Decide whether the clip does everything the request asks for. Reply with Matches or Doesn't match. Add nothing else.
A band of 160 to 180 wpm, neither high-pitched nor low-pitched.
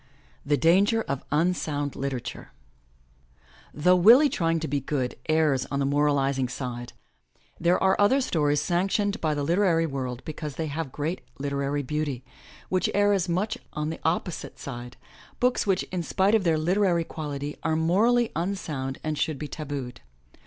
Matches